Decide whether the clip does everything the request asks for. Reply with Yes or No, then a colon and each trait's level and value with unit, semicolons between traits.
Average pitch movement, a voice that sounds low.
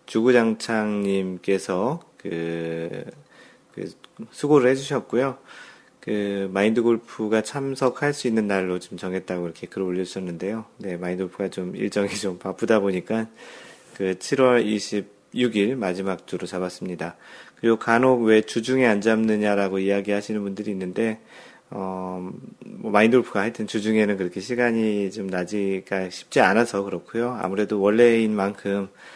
Yes: average, 3.2 semitones; low, 105 Hz